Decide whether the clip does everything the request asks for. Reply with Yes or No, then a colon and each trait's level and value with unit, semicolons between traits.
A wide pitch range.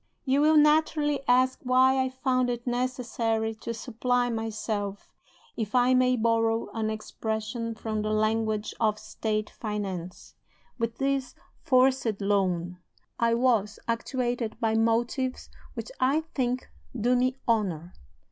No: average, 2.8 semitones